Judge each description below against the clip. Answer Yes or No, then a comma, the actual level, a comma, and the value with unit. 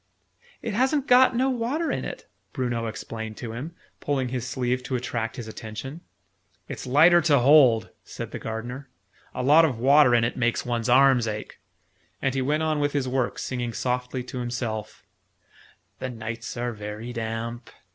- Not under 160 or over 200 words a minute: Yes, average, 170 wpm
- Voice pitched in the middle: No, low, 125 Hz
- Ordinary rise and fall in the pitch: Yes, average, 3.7 semitones